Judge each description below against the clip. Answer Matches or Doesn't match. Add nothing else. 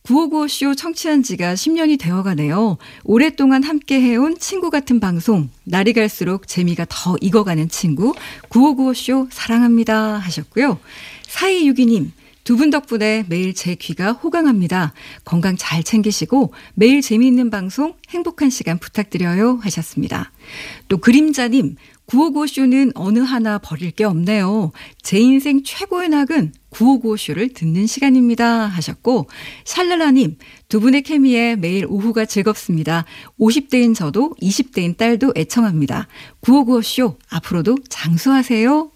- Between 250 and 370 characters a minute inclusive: Matches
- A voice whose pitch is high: Matches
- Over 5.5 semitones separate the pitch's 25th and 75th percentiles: Matches